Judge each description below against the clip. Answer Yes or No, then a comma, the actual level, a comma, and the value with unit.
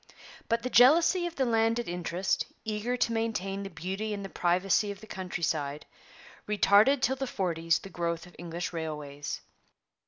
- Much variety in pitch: No, average, 4.9 semitones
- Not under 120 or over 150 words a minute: No, average, 160 wpm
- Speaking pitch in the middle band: No, high, 195 Hz